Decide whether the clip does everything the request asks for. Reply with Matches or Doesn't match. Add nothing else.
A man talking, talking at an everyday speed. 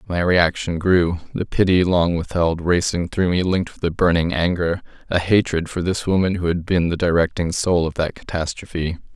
Matches